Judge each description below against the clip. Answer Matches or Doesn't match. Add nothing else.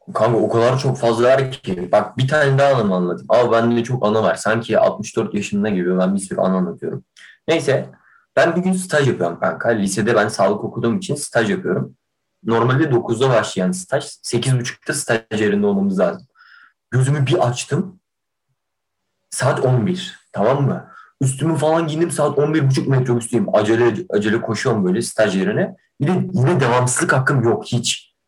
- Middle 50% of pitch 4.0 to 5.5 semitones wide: Matches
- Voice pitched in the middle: Doesn't match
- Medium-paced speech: Doesn't match